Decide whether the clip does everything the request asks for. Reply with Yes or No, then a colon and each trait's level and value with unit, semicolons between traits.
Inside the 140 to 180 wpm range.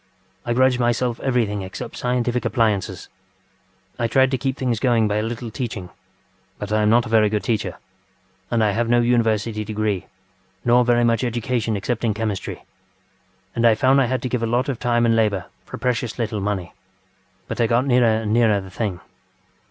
No: average, 190 wpm